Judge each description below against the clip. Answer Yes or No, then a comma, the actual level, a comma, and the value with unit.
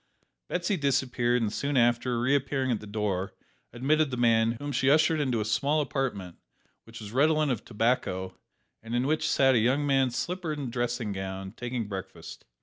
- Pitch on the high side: No, low, 125 Hz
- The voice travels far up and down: No, average, 3.9 semitones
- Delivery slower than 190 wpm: Yes, average, 175 wpm